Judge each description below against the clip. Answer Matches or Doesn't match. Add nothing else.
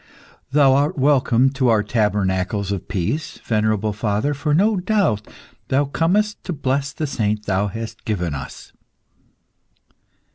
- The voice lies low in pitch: Matches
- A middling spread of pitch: Doesn't match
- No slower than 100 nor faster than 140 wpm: Matches